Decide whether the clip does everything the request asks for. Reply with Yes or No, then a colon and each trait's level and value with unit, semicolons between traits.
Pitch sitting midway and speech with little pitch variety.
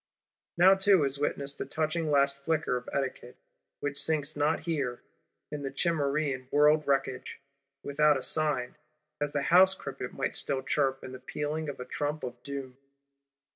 Yes: medium, 145 Hz; narrow, 2.3 semitones